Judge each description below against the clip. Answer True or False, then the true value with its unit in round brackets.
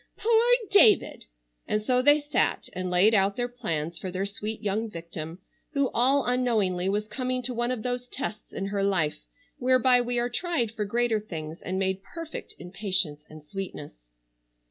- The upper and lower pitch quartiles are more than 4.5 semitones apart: True (5.1 semitones)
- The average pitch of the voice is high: True (215 Hz)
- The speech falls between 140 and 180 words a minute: True (175 wpm)